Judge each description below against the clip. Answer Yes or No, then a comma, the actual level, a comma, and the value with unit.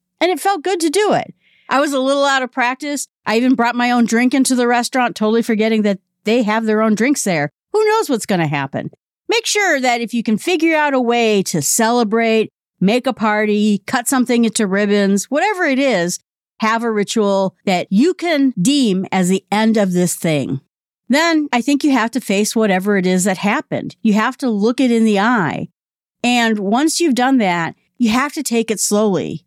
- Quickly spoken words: Yes, fast, 210 wpm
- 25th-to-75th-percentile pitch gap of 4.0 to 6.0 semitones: Yes, average, 4.5 semitones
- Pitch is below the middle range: No, high, 230 Hz